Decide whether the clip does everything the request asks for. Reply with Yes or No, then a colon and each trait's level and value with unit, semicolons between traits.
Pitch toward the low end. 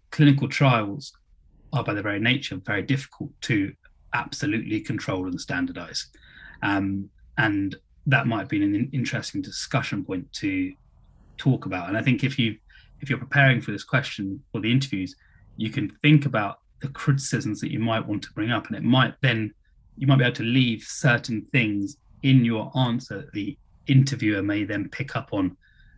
Yes: low, 120 Hz